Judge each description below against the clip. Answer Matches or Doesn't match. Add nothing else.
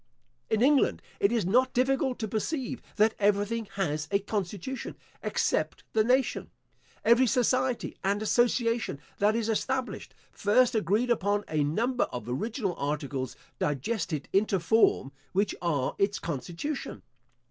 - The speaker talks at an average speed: Doesn't match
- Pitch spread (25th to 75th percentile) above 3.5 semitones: Matches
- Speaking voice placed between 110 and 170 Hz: Doesn't match